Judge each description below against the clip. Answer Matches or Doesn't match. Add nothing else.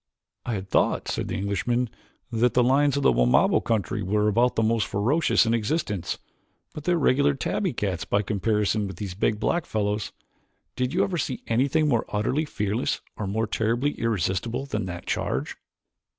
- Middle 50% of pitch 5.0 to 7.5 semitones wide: Doesn't match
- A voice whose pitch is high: Doesn't match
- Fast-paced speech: Doesn't match